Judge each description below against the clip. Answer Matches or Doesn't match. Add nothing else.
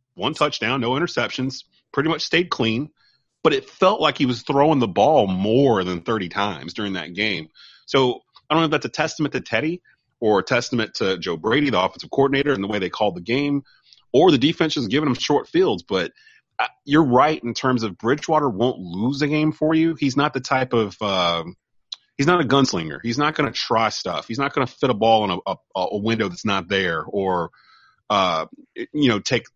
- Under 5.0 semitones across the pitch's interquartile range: Doesn't match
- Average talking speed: Doesn't match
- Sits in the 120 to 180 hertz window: Matches